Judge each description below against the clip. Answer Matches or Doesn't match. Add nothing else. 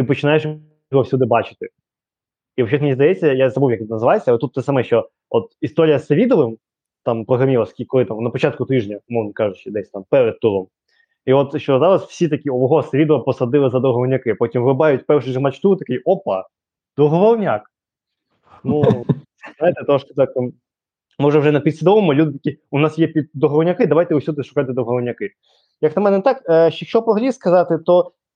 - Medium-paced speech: Doesn't match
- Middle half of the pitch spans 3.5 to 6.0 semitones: Matches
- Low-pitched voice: Doesn't match